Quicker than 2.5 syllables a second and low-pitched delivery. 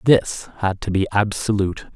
Yes: 5.1 syllables/s; low, 100 Hz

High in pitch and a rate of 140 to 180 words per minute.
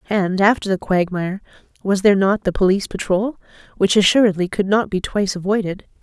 Yes: high, 195 Hz; average, 170 wpm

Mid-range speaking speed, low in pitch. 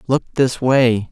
Yes: average, 160 wpm; low, 125 Hz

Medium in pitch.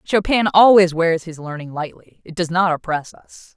Yes: medium, 175 Hz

